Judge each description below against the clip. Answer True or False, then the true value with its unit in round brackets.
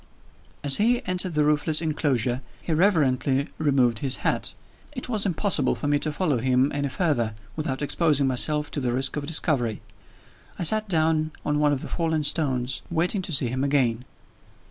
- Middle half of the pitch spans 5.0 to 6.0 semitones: False (3.7 semitones)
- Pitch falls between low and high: True (150 Hz)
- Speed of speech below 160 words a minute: False (175 wpm)